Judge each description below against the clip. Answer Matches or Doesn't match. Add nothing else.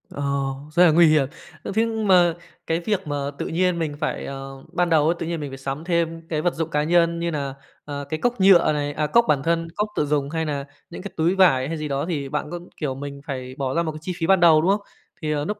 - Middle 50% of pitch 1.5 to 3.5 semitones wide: Matches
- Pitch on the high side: Doesn't match